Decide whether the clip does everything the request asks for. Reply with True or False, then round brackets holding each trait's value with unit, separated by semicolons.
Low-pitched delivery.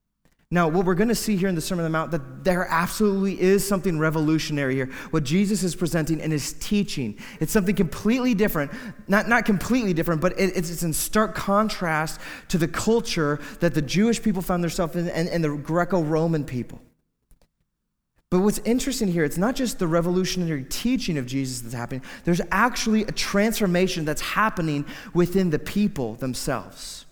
False (175 Hz)